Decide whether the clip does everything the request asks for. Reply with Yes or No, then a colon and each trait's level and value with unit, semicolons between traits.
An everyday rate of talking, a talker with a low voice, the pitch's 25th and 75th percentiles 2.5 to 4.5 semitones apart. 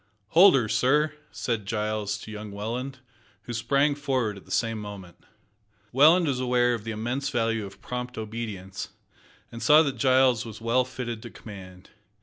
Yes: average, 165 wpm; low, 120 Hz; average, 3.5 semitones